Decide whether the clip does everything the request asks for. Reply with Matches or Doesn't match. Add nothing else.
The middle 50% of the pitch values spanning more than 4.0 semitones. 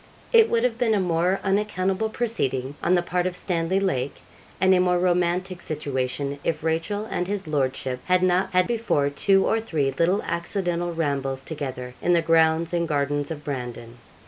Matches